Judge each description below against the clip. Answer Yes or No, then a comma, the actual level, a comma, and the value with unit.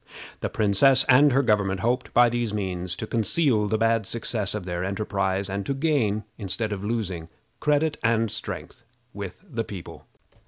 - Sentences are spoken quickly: No, average, 165 wpm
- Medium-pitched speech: No, low, 110 Hz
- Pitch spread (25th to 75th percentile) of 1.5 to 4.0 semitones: Yes, average, 3.6 semitones